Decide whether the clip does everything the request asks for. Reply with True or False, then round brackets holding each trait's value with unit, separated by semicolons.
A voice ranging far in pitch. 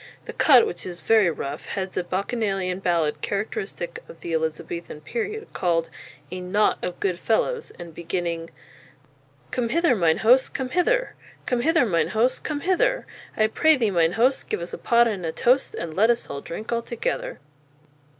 True (6.8 semitones)